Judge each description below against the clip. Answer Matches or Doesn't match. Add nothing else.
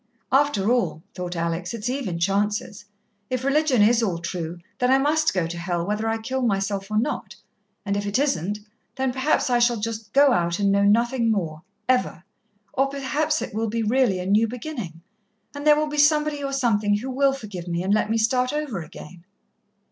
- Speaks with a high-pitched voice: Matches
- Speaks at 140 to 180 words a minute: Doesn't match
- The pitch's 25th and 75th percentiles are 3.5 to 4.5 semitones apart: Doesn't match